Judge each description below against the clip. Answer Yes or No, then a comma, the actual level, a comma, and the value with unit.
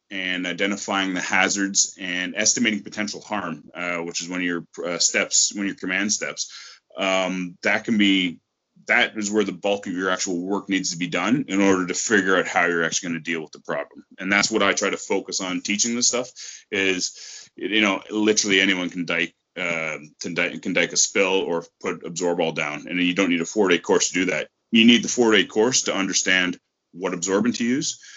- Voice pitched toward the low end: Yes, very low, 95 Hz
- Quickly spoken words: Yes, fast, 225 wpm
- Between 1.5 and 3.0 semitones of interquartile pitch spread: Yes, average, 2.7 semitones